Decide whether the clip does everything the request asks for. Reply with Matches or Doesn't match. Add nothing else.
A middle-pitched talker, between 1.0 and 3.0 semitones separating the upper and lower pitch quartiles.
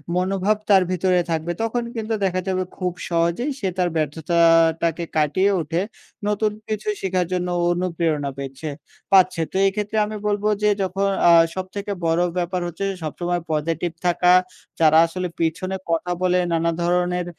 Matches